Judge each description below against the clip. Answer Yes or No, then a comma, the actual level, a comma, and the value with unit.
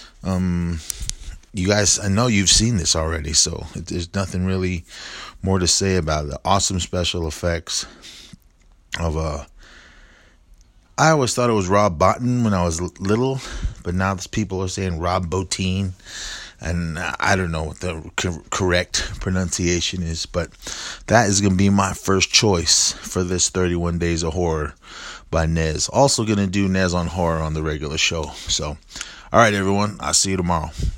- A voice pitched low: Yes, very low, 90 Hz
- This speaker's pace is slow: No, average, 165 wpm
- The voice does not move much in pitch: No, average, 3.0 semitones